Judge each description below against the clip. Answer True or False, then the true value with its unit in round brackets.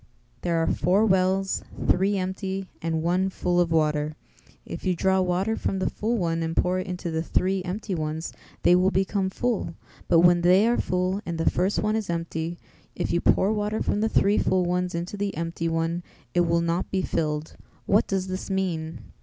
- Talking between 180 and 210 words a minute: True (200 wpm)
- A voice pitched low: False (180 Hz)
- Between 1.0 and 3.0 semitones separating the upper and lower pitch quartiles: True (2.4 semitones)